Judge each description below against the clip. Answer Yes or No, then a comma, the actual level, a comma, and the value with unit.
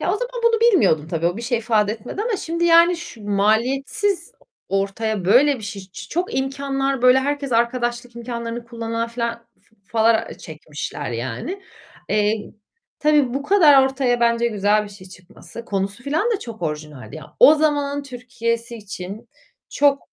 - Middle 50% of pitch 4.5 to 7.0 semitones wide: Yes, average, 5.3 semitones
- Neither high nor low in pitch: No, high, 235 Hz